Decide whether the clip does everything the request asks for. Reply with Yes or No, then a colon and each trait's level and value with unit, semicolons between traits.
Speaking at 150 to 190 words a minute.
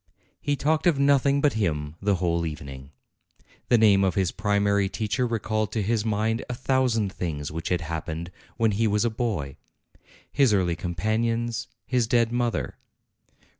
Yes: average, 160 wpm